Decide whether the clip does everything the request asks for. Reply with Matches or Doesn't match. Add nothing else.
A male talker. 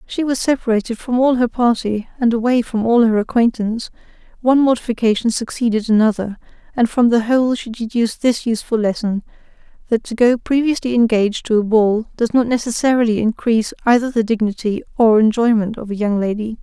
Doesn't match